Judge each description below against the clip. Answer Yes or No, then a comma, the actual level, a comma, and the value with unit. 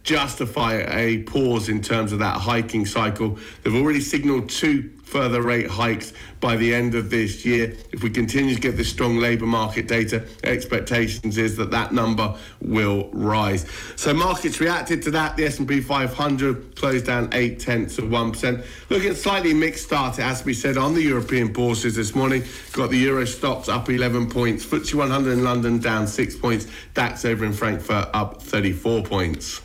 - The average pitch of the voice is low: Yes, low, 120 Hz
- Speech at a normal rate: Yes, average, 180 wpm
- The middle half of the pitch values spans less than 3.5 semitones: Yes, average, 2.9 semitones